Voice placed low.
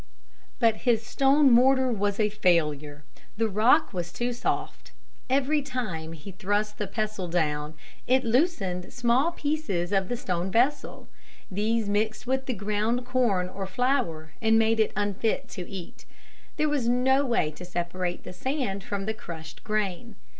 No: high, 215 Hz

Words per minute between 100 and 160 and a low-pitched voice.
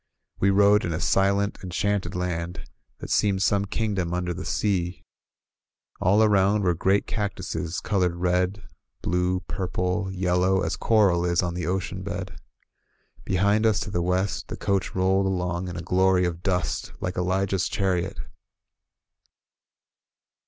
Yes: average, 140 wpm; very low, 95 Hz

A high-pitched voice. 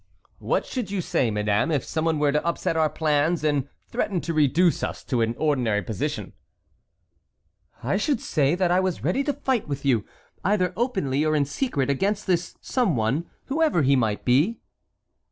No: medium, 155 Hz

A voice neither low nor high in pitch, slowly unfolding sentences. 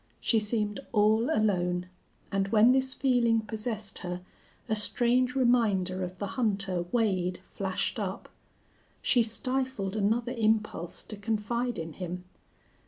No: high, 215 Hz; slow, 125 wpm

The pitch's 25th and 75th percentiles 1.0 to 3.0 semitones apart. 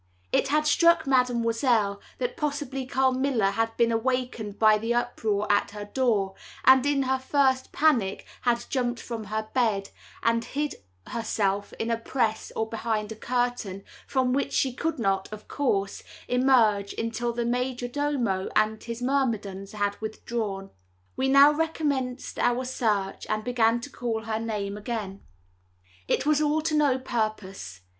No: average, 3.5 semitones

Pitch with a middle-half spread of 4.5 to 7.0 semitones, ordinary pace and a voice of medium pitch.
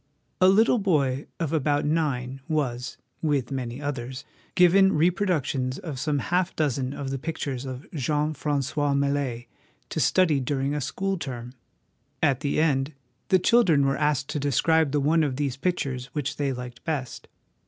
No: average, 3.2 semitones; average, 160 wpm; medium, 145 Hz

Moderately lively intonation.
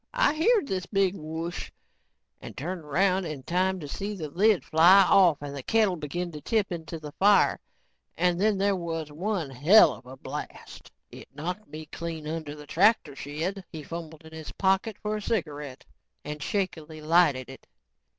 Yes: average, 4.3 semitones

